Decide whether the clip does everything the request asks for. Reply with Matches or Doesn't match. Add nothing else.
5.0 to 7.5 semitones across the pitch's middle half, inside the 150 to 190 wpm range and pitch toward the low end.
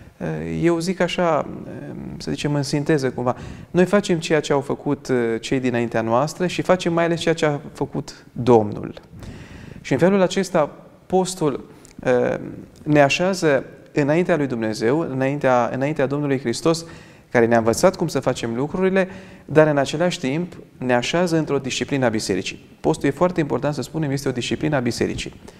Doesn't match